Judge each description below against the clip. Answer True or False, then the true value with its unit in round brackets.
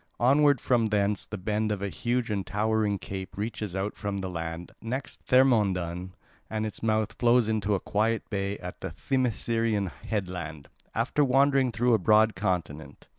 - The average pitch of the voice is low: True (105 Hz)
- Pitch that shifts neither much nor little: True (3.3 semitones)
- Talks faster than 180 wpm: False (165 wpm)